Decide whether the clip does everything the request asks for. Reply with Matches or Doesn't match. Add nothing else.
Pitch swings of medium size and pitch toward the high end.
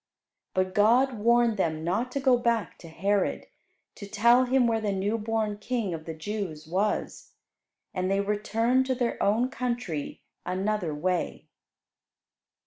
Matches